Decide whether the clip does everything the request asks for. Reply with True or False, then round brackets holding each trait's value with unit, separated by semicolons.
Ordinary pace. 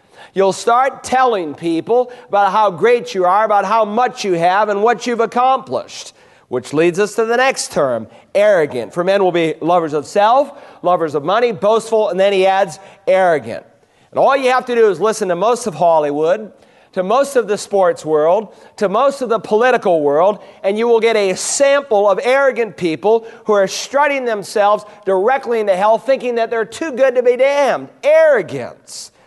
True (185 wpm)